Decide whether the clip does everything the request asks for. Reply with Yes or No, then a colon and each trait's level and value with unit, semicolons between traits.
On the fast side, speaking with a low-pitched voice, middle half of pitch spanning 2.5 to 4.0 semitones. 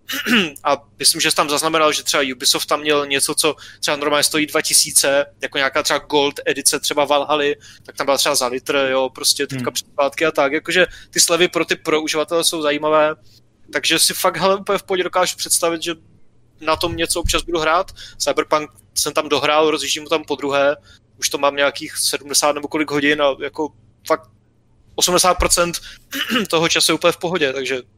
No: fast, 190 wpm; medium, 150 Hz; average, 2.8 semitones